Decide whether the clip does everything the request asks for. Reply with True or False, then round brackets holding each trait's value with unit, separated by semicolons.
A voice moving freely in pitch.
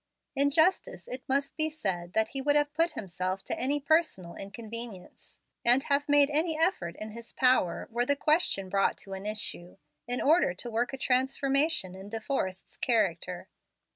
True (6.9 semitones)